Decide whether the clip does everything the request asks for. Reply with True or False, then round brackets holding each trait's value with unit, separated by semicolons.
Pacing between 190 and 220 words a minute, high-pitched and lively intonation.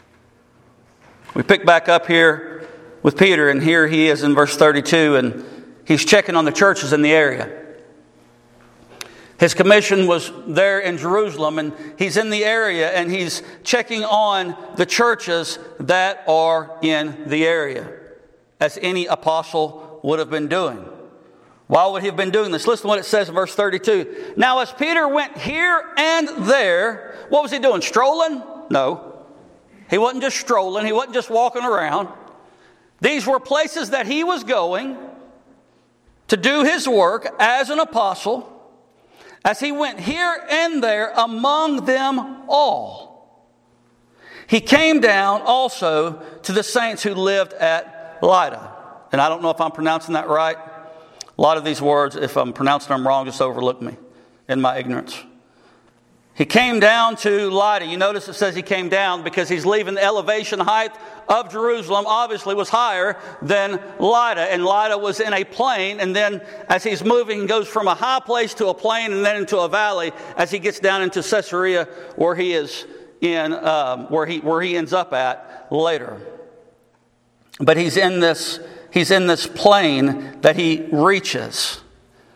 False (165 wpm; 195 Hz; 6.1 semitones)